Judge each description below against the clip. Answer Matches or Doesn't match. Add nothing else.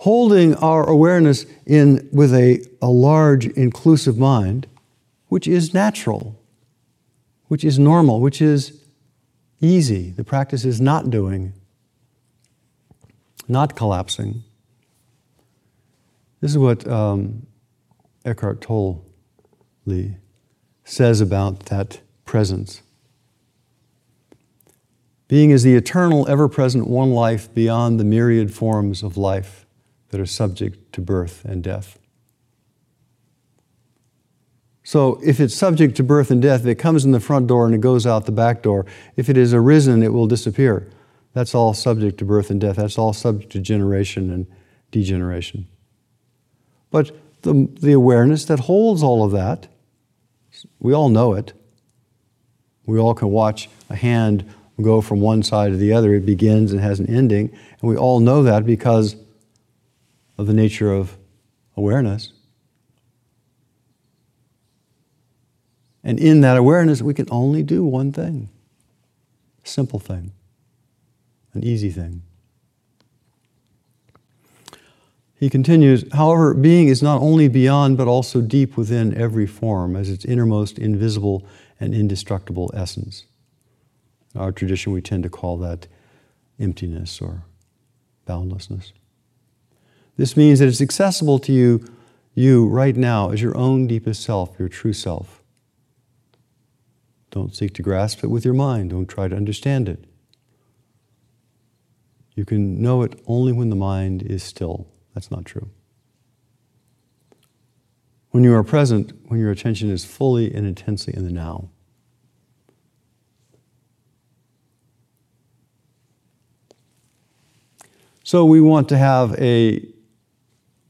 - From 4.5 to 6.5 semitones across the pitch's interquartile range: Doesn't match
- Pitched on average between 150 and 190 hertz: Doesn't match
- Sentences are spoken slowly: Matches